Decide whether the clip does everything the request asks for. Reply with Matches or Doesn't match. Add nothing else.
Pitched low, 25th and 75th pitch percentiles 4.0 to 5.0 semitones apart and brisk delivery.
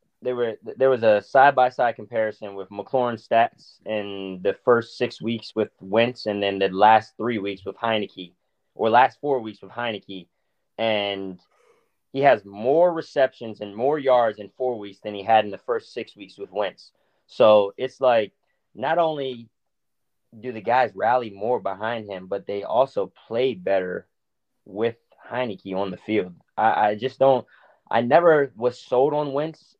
Doesn't match